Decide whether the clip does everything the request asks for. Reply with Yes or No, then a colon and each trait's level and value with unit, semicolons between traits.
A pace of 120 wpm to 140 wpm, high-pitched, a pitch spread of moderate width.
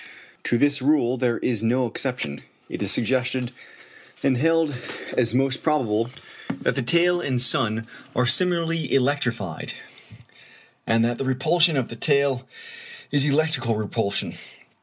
No: slow, 135 wpm; low, 130 Hz; average, 3.8 semitones